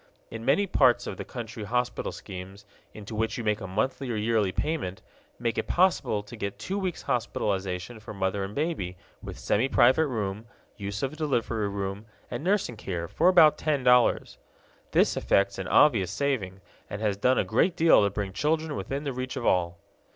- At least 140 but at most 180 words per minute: No, average, 190 wpm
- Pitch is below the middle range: Yes, low, 115 Hz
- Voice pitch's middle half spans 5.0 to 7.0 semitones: Yes, wide, 5.6 semitones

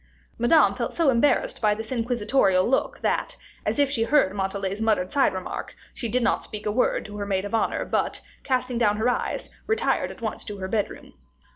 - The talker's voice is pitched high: Yes, high, 225 Hz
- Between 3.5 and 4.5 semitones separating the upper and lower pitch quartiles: Yes, average, 3.8 semitones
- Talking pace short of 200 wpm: No, fast, 205 wpm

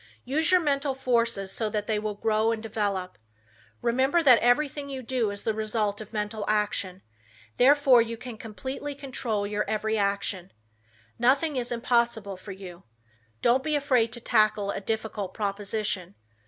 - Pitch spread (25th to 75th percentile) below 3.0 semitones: No, average, 3.6 semitones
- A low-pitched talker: No, high, 225 Hz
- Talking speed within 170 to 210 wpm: No, average, 155 wpm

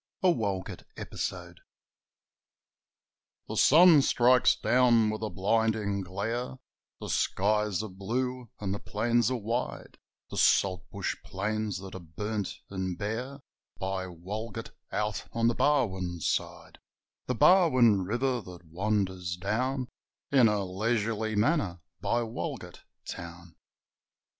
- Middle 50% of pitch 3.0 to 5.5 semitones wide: Yes, average, 4.0 semitones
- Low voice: Yes, low, 105 Hz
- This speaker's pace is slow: Yes, slow, 120 wpm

